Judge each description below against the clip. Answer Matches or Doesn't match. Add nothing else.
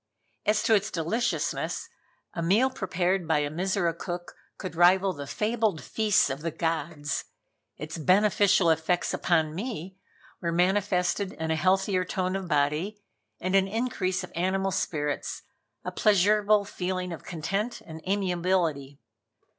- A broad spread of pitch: Doesn't match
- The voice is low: Doesn't match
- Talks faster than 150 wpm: Doesn't match